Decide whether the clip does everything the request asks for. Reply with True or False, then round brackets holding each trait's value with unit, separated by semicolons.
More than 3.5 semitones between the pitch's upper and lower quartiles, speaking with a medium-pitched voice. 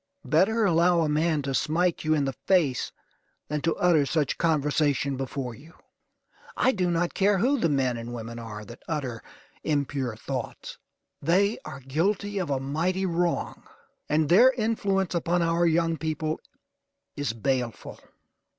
True (4.5 semitones; 155 Hz)